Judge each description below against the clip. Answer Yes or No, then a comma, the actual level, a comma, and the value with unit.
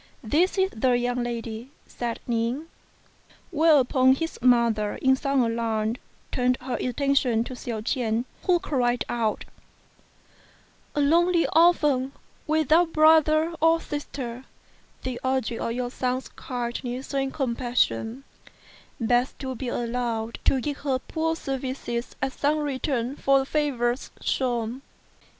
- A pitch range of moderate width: Yes, average, 3.4 semitones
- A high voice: Yes, very high, 255 Hz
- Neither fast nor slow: No, slow, 125 wpm